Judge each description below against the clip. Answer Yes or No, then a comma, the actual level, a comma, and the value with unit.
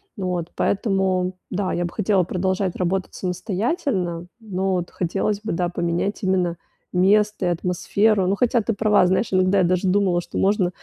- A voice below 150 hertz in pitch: No, medium, 185 Hz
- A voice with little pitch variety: Yes, narrow, 2.1 semitones